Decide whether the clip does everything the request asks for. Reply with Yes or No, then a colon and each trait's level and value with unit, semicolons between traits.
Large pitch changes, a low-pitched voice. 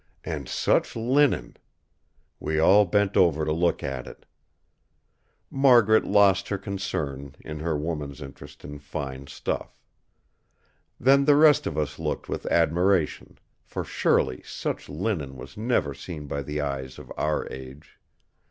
Yes: wide, 6.1 semitones; very low, 80 Hz